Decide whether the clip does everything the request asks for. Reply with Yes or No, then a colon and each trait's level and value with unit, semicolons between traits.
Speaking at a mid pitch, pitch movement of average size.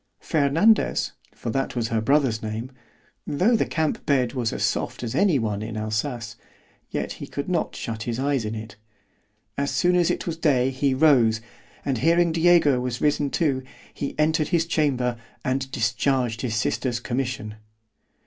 No: low, 130 Hz; average, 4.7 semitones